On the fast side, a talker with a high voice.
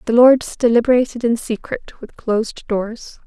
No: average, 145 wpm; high, 235 Hz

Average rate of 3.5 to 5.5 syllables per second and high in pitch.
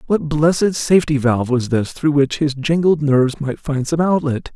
No: 5.0 syllables/s; medium, 145 Hz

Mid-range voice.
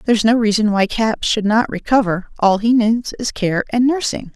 No: high, 220 Hz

